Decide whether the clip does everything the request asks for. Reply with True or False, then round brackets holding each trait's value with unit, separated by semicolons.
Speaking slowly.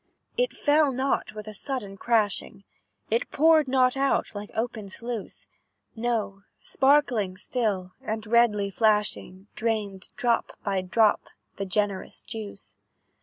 True (120 wpm)